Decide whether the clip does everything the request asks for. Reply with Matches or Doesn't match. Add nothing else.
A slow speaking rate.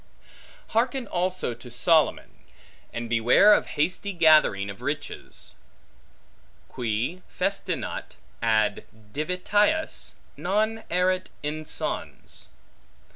Matches